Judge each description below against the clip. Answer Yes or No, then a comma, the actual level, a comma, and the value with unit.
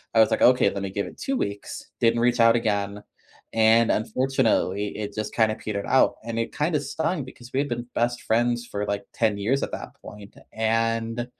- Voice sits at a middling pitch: No, low, 115 Hz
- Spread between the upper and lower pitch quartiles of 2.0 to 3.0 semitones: Yes, narrow, 2.5 semitones